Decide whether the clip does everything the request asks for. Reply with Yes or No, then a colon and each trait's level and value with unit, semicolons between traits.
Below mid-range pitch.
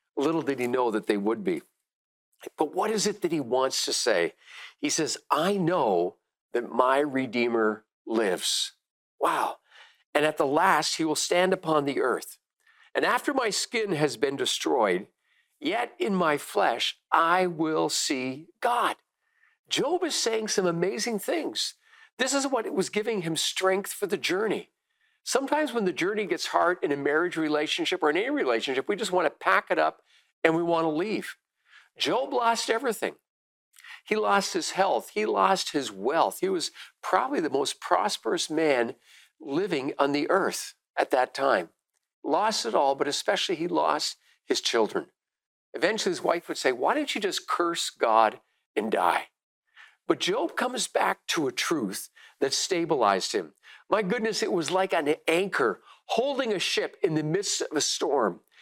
No: high, 225 Hz